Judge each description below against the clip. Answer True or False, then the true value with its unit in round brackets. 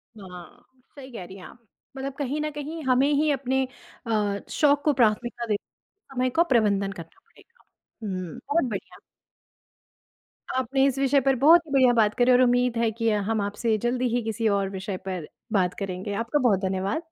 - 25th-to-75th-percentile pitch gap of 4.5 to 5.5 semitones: True (5.0 semitones)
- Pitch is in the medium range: False (240 Hz)